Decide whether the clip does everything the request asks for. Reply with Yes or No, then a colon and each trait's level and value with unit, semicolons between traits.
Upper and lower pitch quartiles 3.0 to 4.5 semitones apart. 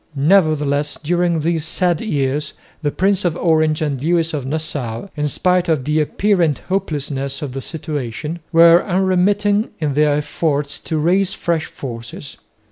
Yes: average, 3.3 semitones